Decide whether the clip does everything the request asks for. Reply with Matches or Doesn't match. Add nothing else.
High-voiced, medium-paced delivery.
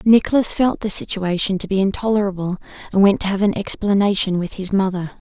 Matches